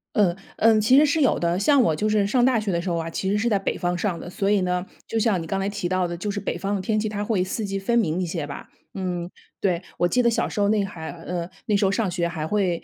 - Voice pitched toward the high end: Yes, high, 195 Hz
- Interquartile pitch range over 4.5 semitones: No, average, 3.3 semitones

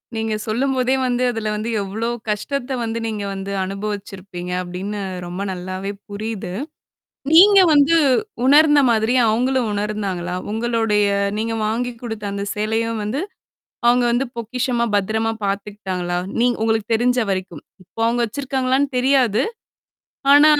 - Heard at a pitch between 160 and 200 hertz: No, high, 220 Hz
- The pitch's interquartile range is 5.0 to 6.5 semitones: No, average, 3.6 semitones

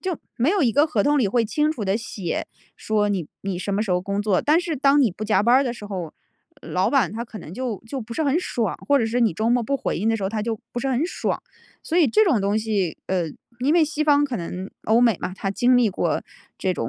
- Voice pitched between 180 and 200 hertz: No, high, 225 Hz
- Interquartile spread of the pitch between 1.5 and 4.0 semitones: No, wide, 5.5 semitones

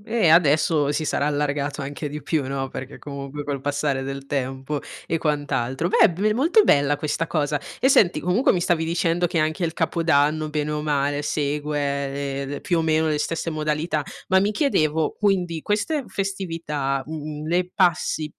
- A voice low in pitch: No, medium, 150 Hz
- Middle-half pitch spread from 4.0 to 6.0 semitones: No, average, 2.8 semitones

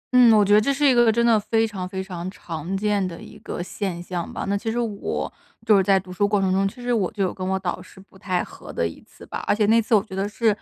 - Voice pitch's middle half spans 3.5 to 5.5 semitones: No, average, 2.8 semitones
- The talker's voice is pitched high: Yes, high, 200 Hz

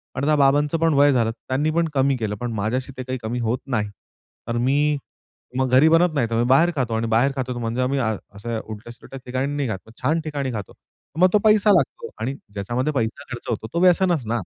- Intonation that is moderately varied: Yes, average, 4.1 semitones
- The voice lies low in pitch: Yes, low, 130 Hz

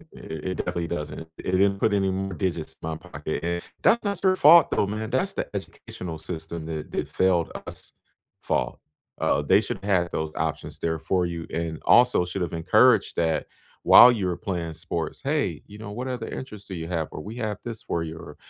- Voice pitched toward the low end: Yes, very low, 90 Hz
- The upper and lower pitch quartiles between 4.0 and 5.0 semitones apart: Yes, average, 4.5 semitones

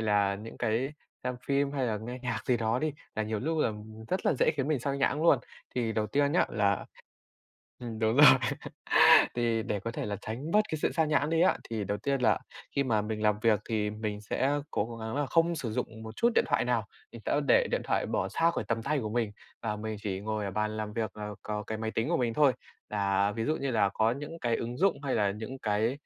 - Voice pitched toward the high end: No, low, 115 Hz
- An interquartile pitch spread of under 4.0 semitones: No, average, 4.5 semitones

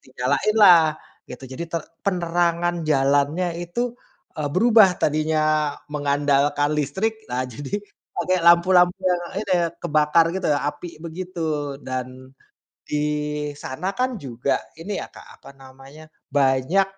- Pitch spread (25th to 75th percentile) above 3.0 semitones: Yes, average, 4.0 semitones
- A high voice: No, medium, 155 Hz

